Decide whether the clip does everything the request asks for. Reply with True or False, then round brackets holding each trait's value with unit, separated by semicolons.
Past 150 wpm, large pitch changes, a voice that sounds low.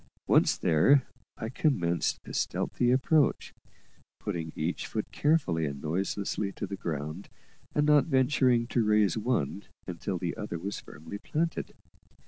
False (135 wpm; 7.6 semitones; 105 Hz)